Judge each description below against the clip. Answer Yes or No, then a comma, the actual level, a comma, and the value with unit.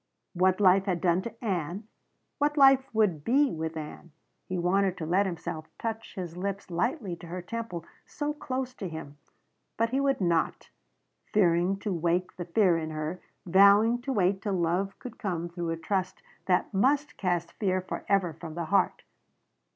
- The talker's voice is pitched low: No, medium, 185 Hz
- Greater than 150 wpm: Yes, average, 175 wpm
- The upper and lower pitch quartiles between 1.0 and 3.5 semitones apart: No, average, 4.1 semitones